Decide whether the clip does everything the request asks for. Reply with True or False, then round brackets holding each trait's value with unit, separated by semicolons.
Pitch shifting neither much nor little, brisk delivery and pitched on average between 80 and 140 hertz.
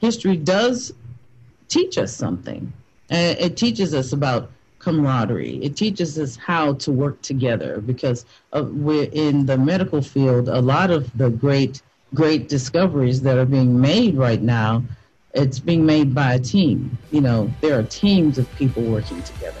False (3.8 semitones; 155 wpm; 135 Hz)